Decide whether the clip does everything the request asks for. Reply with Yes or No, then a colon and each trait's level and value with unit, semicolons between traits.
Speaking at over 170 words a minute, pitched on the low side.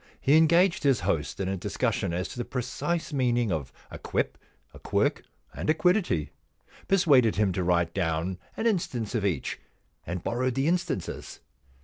No: average, 165 wpm; low, 120 Hz